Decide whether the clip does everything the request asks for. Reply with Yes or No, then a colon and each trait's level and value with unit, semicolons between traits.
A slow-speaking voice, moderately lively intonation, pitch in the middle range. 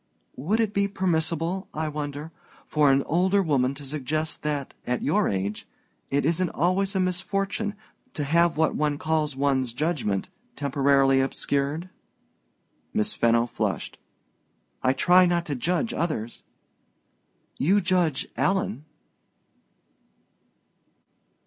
Yes: slow, 120 wpm; average, 4.6 semitones; medium, 155 Hz